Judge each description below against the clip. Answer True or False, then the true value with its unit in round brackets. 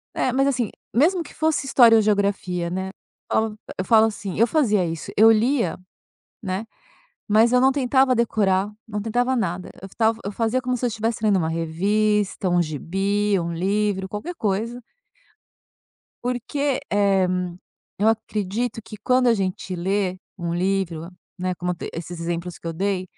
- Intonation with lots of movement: False (4.1 semitones)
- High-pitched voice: True (205 Hz)